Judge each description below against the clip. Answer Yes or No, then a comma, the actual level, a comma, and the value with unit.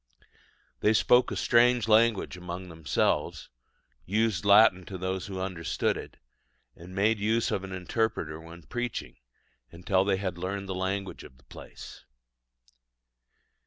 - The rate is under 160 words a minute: Yes, slow, 135 wpm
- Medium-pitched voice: No, very low, 95 Hz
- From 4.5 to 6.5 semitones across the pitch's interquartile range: No, average, 3.3 semitones